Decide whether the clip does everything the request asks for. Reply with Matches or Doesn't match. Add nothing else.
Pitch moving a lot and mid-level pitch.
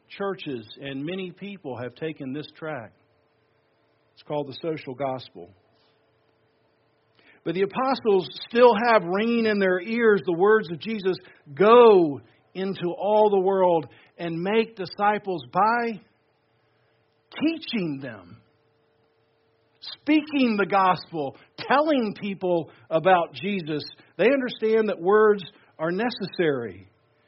Matches